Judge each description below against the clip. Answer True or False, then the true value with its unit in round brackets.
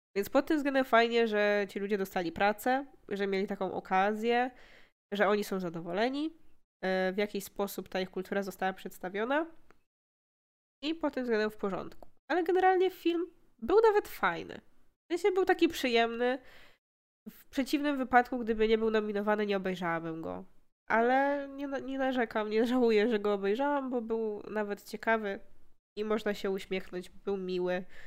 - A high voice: True (215 Hz)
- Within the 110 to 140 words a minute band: False (155 wpm)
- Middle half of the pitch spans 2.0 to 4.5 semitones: False (5.0 semitones)